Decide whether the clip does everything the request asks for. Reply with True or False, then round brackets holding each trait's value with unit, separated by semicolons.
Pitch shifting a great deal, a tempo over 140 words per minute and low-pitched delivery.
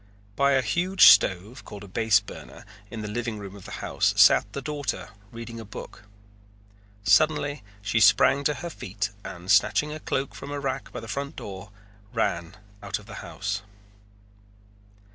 True (5.7 semitones; 170 wpm; 115 Hz)